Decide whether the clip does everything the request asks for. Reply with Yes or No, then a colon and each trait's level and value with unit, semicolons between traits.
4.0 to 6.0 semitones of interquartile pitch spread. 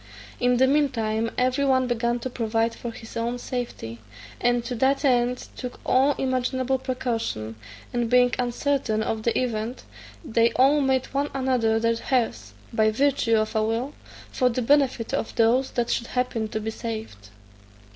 No: narrow, 2.4 semitones